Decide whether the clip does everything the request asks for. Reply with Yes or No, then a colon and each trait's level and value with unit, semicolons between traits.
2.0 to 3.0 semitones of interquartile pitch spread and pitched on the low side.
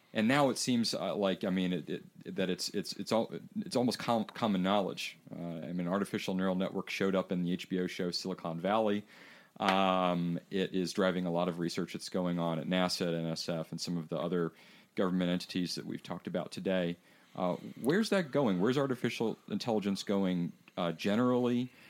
Yes: narrow, 2.5 semitones; very low, 95 Hz